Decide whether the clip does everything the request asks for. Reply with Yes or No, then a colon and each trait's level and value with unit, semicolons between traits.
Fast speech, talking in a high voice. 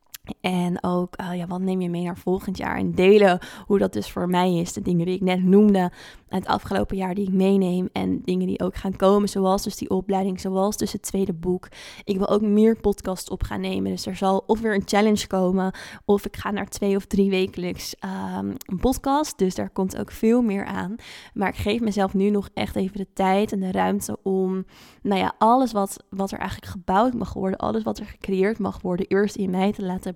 Yes: fast, 230 wpm; high, 195 Hz